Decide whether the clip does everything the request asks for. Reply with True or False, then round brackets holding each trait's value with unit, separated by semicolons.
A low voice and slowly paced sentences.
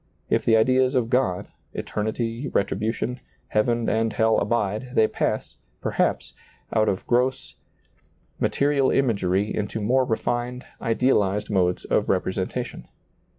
True (115 Hz; 120 wpm)